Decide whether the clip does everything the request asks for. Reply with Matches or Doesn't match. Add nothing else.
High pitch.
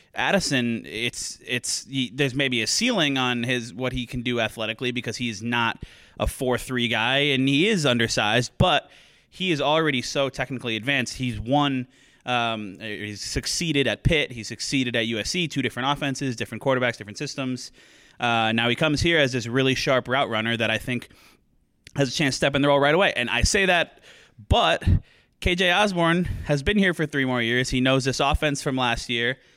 Doesn't match